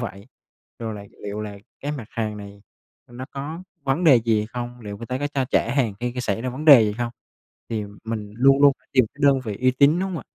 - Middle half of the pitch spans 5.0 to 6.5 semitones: No, average, 4.3 semitones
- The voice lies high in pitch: No, low, 120 Hz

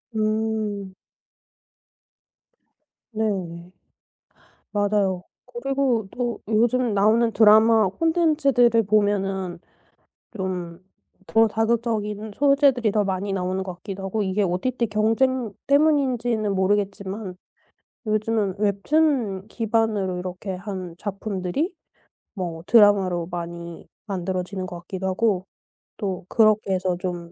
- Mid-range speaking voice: No, high, 205 Hz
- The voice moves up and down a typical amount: Yes, average, 3.3 semitones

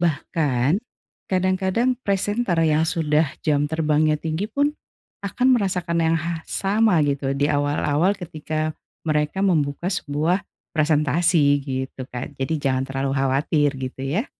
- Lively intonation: No, average, 4.0 semitones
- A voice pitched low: No, medium, 155 Hz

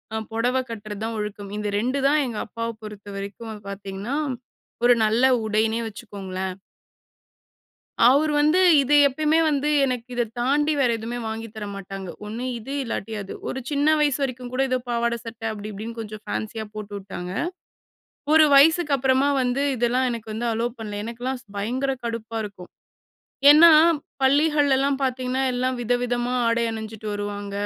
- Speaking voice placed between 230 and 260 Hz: Yes, high, 235 Hz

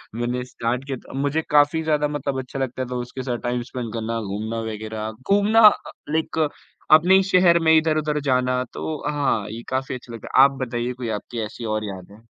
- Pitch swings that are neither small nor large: Yes, average, 4.4 semitones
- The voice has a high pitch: No, low, 125 Hz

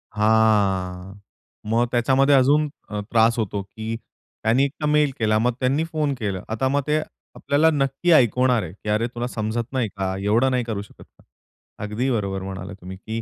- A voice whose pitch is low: Yes, low, 115 Hz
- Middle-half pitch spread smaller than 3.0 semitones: No, average, 4.3 semitones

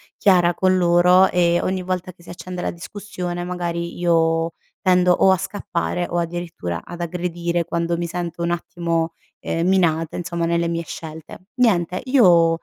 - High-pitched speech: No, medium, 175 Hz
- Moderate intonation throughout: No, narrow, 1.2 semitones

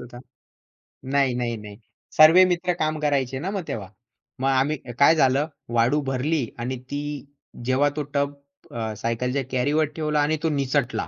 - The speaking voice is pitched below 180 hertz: Yes, medium, 140 Hz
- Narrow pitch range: No, average, 3.3 semitones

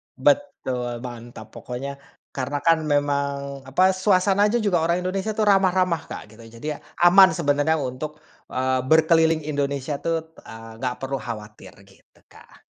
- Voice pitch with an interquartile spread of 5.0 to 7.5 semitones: Yes, wide, 5.4 semitones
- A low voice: No, medium, 145 Hz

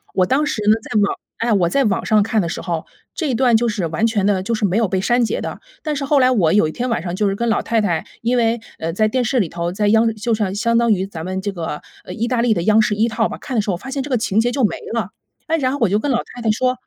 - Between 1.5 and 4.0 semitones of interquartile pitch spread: Yes, average, 3.7 semitones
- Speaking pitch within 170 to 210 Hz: No, high, 220 Hz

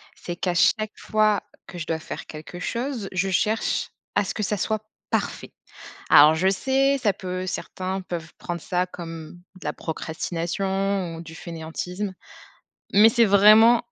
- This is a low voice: No, medium, 185 Hz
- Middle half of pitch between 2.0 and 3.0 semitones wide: No, average, 3.8 semitones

